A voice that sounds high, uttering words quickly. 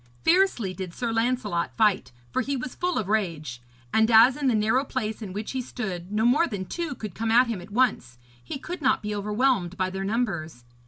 Yes: high, 220 Hz; fast, 215 wpm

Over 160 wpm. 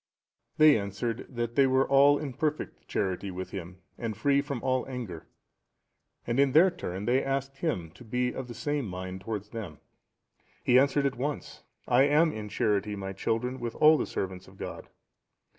Yes: average, 180 wpm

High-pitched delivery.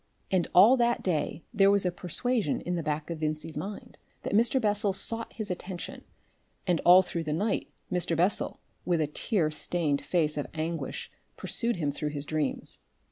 No: medium, 175 Hz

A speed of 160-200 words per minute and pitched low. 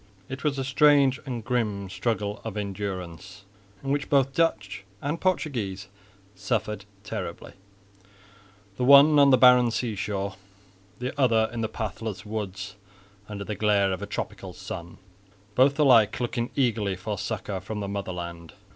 No: average, 145 wpm; low, 110 Hz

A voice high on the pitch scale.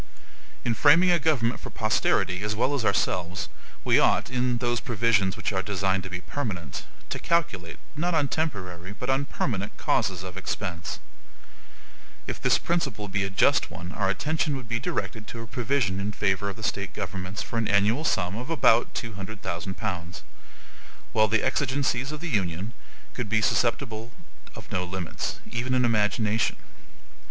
No: low, 110 Hz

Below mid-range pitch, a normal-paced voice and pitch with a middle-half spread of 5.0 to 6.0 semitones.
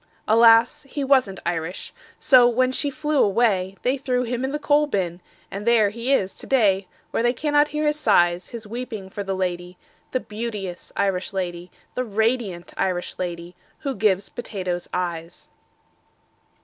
No: high, 215 Hz; average, 160 wpm; wide, 5.6 semitones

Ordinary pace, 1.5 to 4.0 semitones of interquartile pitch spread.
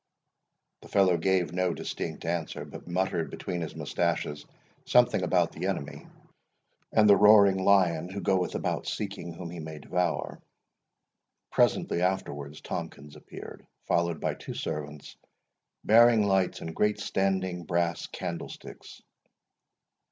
No: slow, 125 wpm; average, 2.8 semitones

